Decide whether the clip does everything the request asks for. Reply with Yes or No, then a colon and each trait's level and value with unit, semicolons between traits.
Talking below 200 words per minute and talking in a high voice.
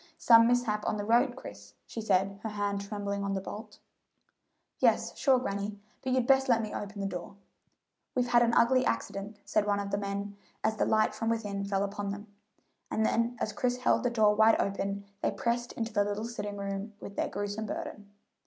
No: fast, 205 wpm; high, 210 Hz